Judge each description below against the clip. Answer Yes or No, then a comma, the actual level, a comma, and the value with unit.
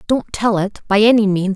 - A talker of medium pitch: No, high, 205 Hz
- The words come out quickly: Yes, fast, 230 wpm